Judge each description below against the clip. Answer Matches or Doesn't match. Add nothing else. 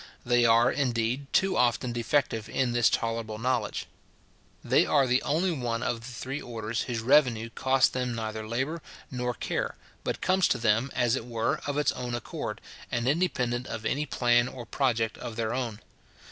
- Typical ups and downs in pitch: Doesn't match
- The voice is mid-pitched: Doesn't match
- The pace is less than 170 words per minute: Doesn't match